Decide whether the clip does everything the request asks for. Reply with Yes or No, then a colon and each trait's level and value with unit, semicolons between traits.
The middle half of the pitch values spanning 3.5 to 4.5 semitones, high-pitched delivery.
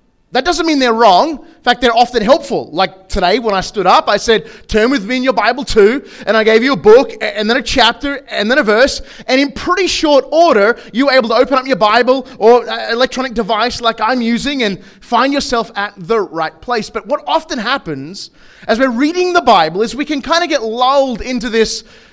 Yes: average, 3.8 semitones; high, 245 Hz